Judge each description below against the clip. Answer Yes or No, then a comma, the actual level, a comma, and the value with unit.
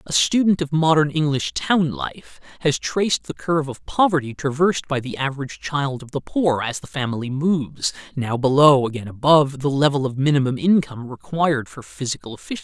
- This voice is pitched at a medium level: Yes, medium, 145 Hz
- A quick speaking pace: No, average, 180 wpm